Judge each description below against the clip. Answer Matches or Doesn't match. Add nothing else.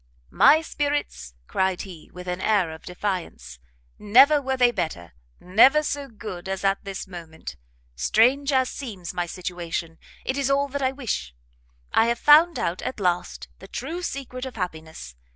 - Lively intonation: Matches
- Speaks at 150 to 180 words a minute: Matches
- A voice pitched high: Matches